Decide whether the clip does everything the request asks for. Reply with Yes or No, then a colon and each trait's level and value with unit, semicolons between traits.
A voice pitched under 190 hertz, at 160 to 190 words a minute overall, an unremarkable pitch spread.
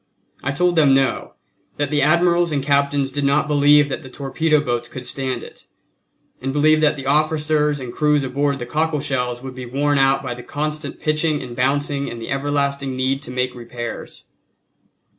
No: medium, 140 Hz; average, 185 wpm; narrow, 2.3 semitones